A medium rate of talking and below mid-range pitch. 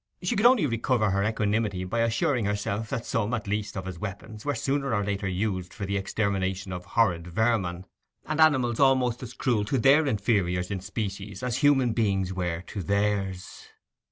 Yes: average, 185 wpm; low, 105 Hz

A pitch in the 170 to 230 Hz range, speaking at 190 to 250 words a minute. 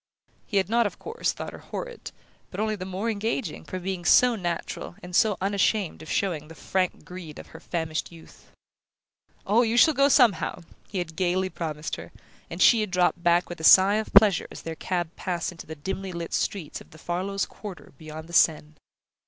Yes: medium, 185 Hz; average, 200 wpm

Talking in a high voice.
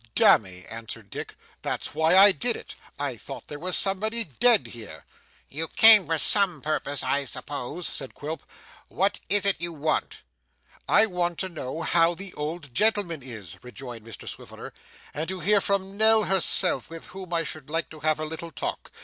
No: medium, 165 Hz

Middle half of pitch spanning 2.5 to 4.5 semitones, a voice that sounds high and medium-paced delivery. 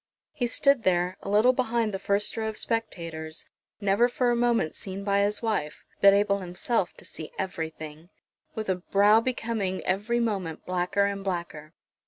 Yes: average, 4.1 semitones; high, 200 Hz; average, 170 wpm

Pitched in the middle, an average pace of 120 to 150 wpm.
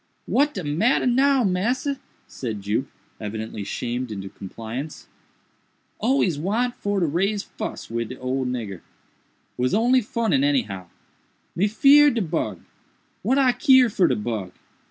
Yes: medium, 170 Hz; average, 140 wpm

